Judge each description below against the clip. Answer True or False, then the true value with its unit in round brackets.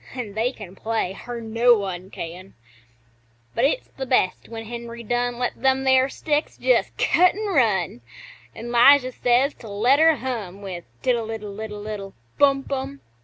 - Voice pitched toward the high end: True (235 Hz)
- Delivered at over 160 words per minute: True (170 wpm)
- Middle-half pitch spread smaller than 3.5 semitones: False (4.1 semitones)